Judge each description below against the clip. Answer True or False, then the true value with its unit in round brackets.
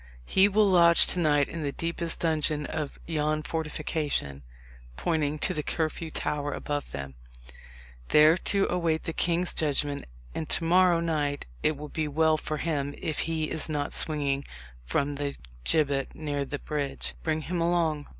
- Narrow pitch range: True (2.2 semitones)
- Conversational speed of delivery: True (160 wpm)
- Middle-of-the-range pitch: True (155 Hz)